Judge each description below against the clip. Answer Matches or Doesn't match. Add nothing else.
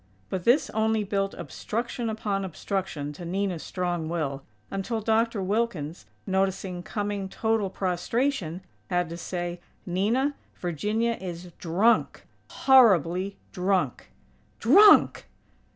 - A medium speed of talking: Doesn't match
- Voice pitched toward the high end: Matches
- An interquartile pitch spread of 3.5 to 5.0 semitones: Matches